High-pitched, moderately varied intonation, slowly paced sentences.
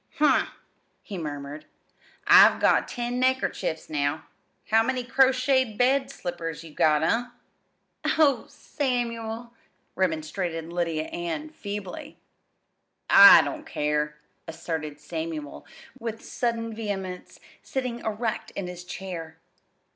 No: high, 195 Hz; wide, 7.0 semitones; slow, 105 wpm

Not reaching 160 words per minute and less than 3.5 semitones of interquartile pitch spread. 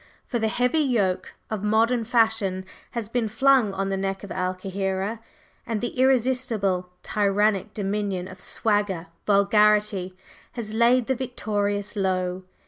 Yes: slow, 135 wpm; average, 3.1 semitones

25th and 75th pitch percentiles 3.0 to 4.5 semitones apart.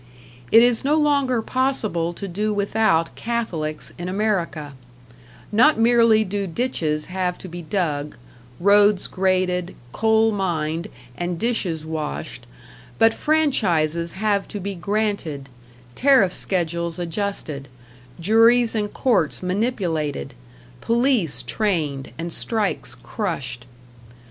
No: average, 5.1 semitones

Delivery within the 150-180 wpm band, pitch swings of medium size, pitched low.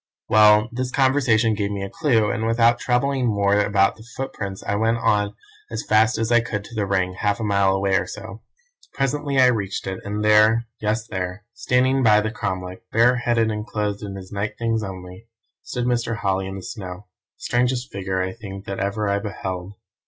No: average, 195 wpm; average, 3.0 semitones; low, 105 Hz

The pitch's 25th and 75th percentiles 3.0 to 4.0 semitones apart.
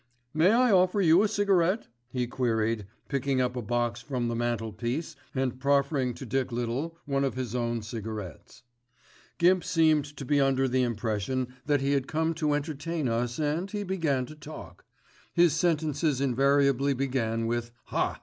No: average, 4.6 semitones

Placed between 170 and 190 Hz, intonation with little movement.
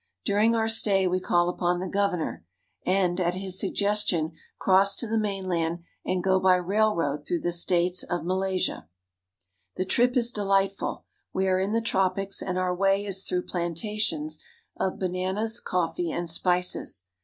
Yes: medium, 185 Hz; narrow, 2.1 semitones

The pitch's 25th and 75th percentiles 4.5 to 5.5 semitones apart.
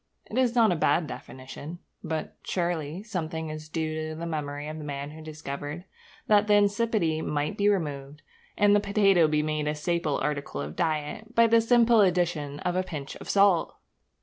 Yes: average, 5.0 semitones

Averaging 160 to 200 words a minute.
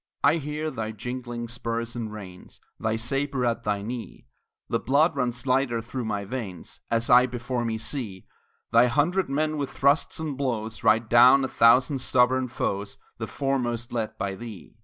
Yes: average, 170 wpm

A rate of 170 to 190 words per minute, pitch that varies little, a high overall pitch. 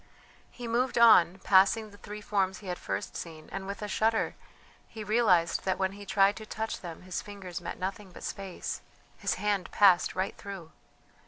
Yes: average, 185 wpm; narrow, 2.3 semitones; high, 195 Hz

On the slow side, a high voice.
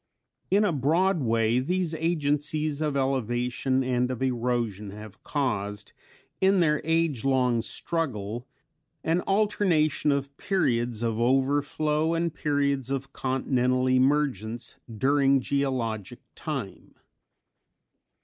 No: slow, 110 wpm; low, 135 Hz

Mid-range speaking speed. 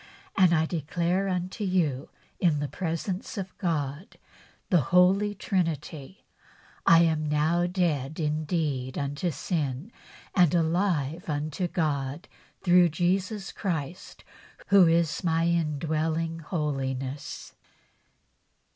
No: slow, 100 wpm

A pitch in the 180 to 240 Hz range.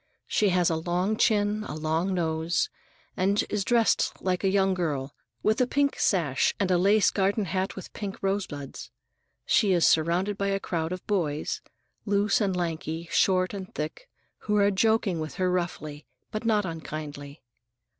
Yes: medium, 185 Hz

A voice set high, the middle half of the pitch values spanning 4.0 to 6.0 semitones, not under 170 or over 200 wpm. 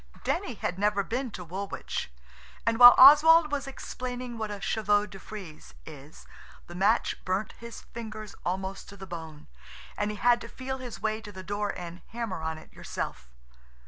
Yes: high, 210 Hz; average, 4.3 semitones; average, 175 wpm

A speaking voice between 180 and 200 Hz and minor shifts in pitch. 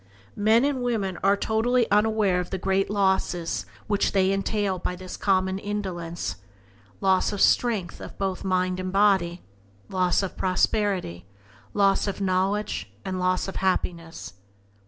Yes: high, 190 Hz; narrow, 2.0 semitones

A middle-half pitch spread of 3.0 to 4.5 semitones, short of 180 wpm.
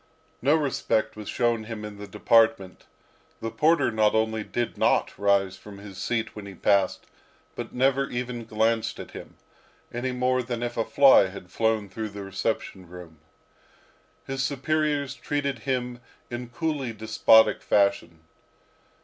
Yes: average, 3.8 semitones; average, 150 wpm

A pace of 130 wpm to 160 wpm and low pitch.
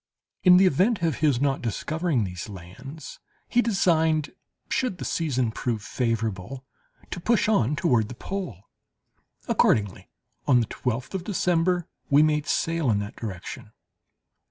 No: average, 140 wpm; medium, 145 Hz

